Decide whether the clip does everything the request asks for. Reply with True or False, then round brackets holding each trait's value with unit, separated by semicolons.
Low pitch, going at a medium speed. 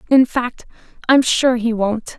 False (240 Hz; 165 wpm)